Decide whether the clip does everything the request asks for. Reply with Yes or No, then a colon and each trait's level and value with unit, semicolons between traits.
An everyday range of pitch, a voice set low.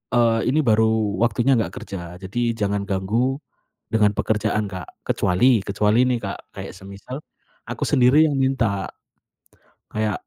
Yes: average, 3.6 semitones; low, 110 Hz